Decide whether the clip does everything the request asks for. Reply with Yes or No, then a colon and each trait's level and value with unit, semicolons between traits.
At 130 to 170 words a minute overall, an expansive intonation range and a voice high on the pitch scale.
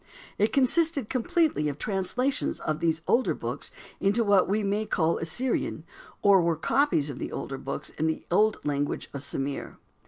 Yes: average, 165 wpm; wide, 7.2 semitones; high, 195 Hz